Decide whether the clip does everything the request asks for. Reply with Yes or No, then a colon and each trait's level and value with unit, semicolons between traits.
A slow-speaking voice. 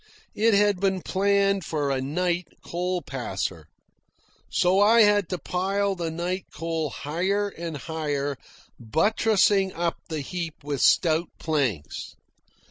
Yes: slow, 130 wpm